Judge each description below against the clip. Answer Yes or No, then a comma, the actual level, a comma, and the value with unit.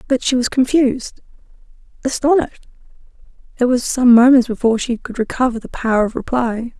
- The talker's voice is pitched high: Yes, high, 245 Hz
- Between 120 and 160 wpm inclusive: Yes, average, 140 wpm